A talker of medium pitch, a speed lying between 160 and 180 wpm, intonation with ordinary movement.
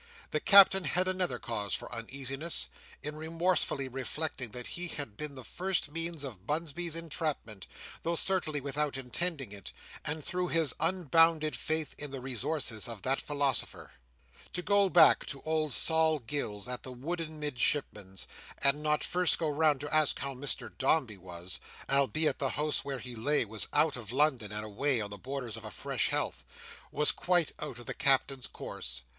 Yes: medium, 145 Hz; average, 170 wpm; average, 4.4 semitones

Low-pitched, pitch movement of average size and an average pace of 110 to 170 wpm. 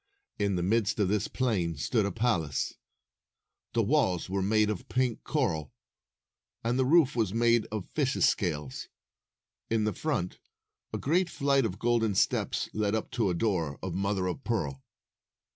Yes: low, 105 Hz; average, 4.7 semitones; average, 160 wpm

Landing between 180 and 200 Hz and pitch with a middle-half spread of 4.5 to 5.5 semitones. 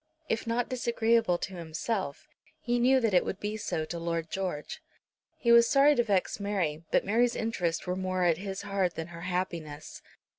Yes: high, 190 Hz; average, 5.1 semitones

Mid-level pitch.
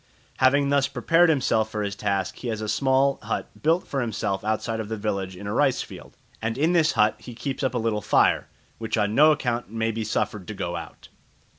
No: low, 115 Hz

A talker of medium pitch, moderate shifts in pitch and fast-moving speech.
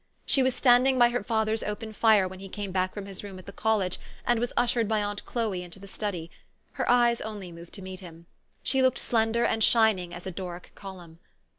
No: high, 205 Hz; average, 3.6 semitones; fast, 225 wpm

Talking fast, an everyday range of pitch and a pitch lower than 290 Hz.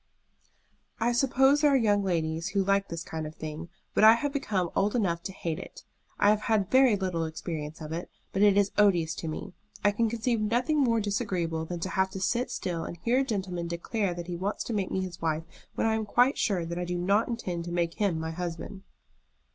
Yes: fast, 230 wpm; average, 4.5 semitones; high, 190 Hz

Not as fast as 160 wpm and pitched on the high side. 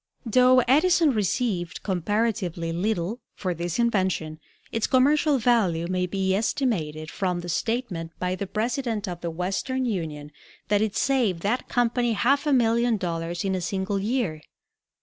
Yes: average, 150 wpm; high, 205 Hz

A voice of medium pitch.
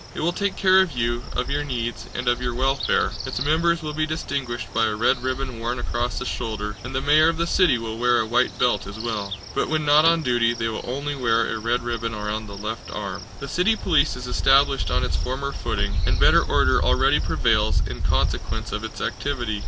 No: low, 125 Hz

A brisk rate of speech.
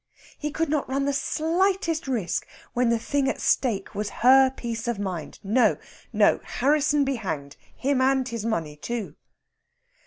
No: average, 160 wpm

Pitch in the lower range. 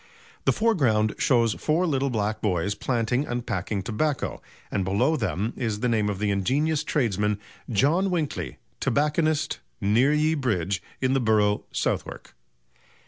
Yes: low, 120 Hz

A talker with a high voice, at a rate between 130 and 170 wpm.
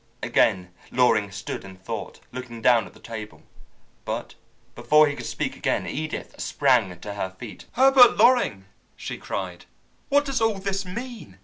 No: low, 125 Hz; average, 155 wpm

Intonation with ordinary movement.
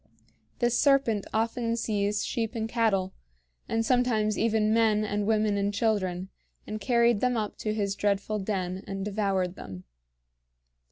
No: narrow, 2.2 semitones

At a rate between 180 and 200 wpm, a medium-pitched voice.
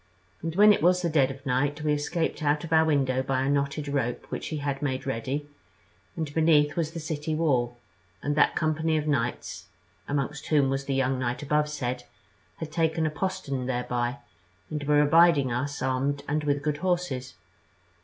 Yes: average, 185 wpm; medium, 145 Hz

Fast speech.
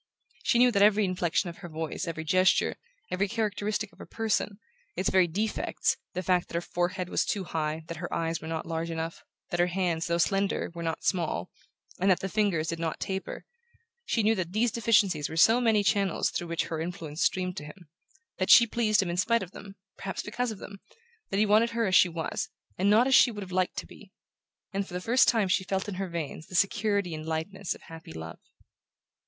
Yes: fast, 225 wpm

